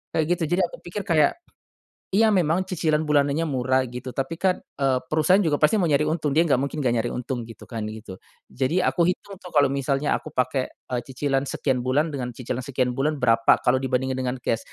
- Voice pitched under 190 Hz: Yes, medium, 140 Hz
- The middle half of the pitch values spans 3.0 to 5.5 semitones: Yes, average, 3.5 semitones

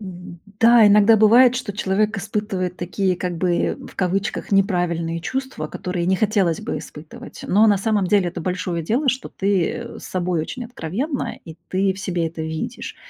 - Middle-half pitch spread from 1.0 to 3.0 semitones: No, average, 3.6 semitones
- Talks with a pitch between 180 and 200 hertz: Yes, high, 190 Hz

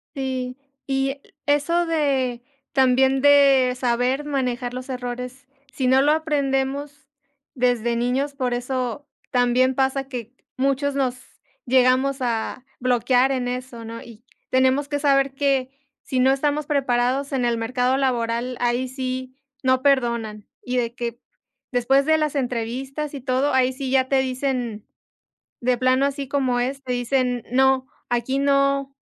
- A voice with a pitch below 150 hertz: No, very high, 260 Hz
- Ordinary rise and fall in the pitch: No, narrow, 1.8 semitones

